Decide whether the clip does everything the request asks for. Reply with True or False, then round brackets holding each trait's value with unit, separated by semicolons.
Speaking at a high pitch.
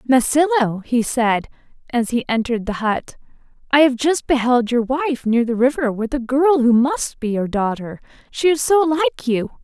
True (250 Hz)